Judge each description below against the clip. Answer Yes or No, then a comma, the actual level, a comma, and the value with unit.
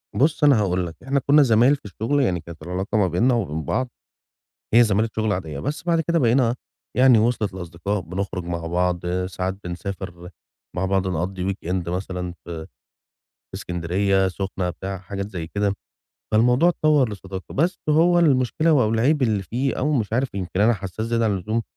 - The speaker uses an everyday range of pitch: No, wide, 5.7 semitones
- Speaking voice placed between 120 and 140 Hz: No, low, 100 Hz